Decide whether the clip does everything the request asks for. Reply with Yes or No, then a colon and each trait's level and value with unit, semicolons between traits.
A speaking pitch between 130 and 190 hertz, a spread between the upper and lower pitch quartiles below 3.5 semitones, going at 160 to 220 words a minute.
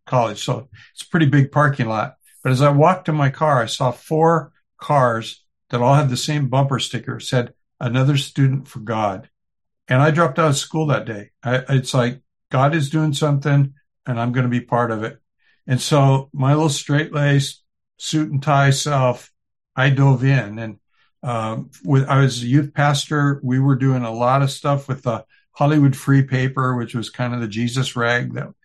Yes: low, 135 Hz; average, 2.8 semitones; average, 200 wpm